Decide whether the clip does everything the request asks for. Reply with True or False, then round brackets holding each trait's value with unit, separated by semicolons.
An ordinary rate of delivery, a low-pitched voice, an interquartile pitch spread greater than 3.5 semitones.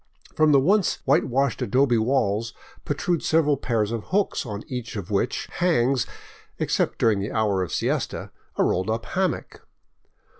True (155 wpm; 120 Hz; 5.2 semitones)